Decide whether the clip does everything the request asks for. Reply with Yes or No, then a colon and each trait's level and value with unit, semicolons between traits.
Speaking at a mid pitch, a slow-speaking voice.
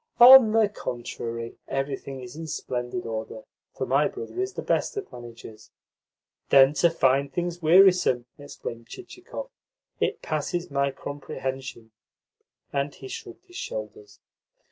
Yes: medium, 145 Hz; slow, 130 wpm